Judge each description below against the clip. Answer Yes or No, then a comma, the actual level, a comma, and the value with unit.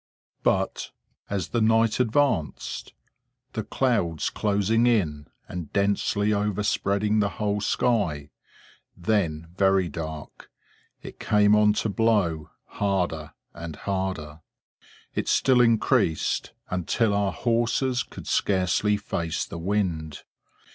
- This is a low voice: Yes, low, 100 Hz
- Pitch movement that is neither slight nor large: Yes, average, 4.4 semitones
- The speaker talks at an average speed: No, slow, 105 wpm